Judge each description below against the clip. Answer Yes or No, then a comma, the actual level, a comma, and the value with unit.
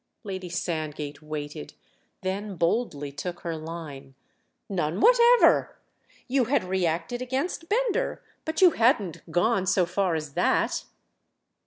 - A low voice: No, medium, 185 Hz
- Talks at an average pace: No, slow, 110 wpm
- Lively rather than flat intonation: Yes, wide, 7.6 semitones